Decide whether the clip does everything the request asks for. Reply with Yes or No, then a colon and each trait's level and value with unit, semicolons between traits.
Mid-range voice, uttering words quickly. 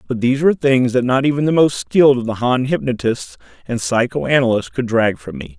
No: low, 120 Hz; fast, 215 wpm